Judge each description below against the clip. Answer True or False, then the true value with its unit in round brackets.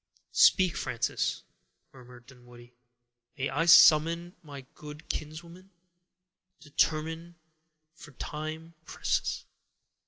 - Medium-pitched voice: True (155 Hz)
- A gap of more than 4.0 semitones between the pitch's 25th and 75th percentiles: False (3.6 semitones)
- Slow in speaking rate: True (85 wpm)